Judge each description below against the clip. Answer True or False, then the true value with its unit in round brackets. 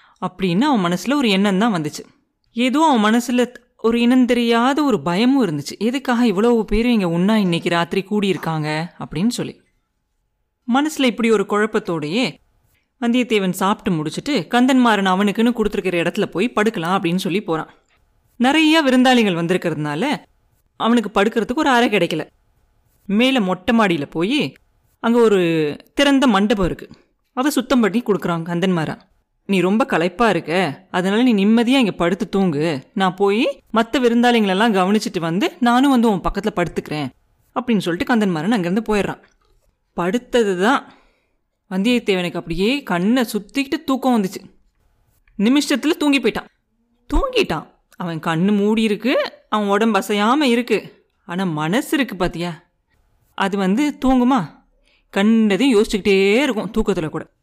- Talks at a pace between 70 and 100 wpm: False (125 wpm)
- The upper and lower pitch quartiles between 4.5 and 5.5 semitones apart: True (5.0 semitones)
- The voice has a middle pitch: False (210 Hz)